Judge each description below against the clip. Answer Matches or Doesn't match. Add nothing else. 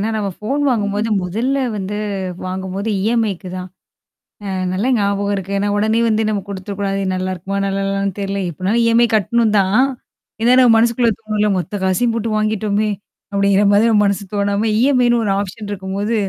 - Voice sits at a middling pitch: Doesn't match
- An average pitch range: Doesn't match